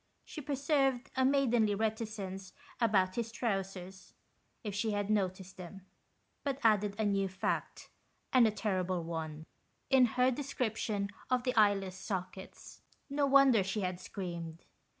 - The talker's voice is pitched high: Yes, high, 210 Hz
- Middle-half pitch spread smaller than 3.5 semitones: No, average, 4.4 semitones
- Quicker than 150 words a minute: No, slow, 135 wpm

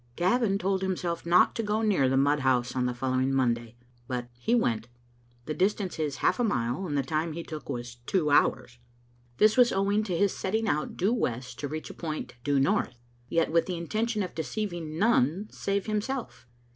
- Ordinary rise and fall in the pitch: No, wide, 7.2 semitones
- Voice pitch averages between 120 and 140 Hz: No, medium, 165 Hz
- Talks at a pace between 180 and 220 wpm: Yes, average, 200 wpm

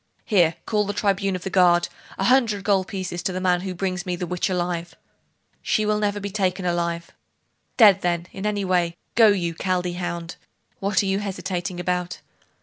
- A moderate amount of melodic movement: No, narrow, 2.3 semitones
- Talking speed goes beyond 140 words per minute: Yes, average, 190 wpm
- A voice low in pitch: No, medium, 185 Hz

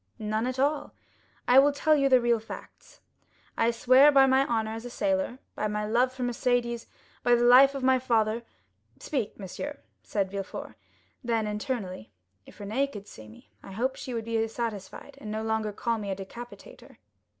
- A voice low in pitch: No, high, 235 Hz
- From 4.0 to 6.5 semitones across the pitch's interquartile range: No, average, 3.3 semitones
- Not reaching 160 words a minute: No, average, 185 wpm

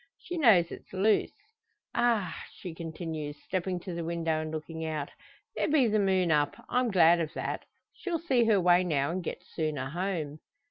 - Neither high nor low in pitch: Yes, medium, 175 Hz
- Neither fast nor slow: Yes, average, 180 wpm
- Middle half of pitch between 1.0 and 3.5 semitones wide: No, average, 4.2 semitones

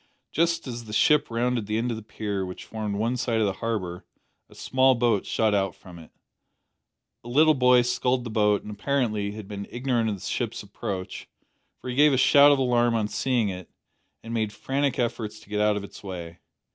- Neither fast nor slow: No, fast, 210 wpm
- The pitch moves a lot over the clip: No, average, 3.5 semitones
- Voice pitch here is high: No, low, 115 Hz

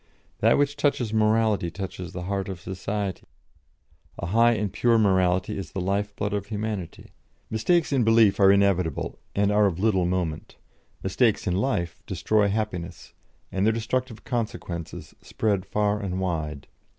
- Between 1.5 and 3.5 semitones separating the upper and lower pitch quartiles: Yes, average, 3.1 semitones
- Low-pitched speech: Yes, low, 100 Hz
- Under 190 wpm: Yes, average, 150 wpm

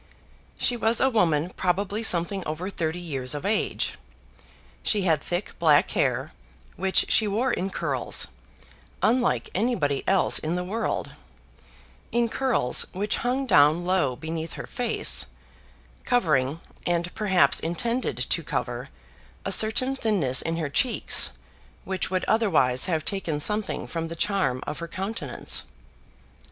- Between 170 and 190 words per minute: No, slow, 135 wpm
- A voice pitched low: No, medium, 180 Hz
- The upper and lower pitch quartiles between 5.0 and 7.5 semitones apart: Yes, wide, 5.5 semitones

